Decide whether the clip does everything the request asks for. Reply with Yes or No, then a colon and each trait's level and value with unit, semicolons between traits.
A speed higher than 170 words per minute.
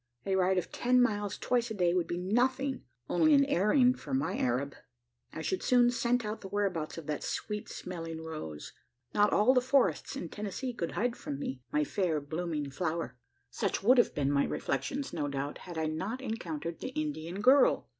Yes: average, 195 wpm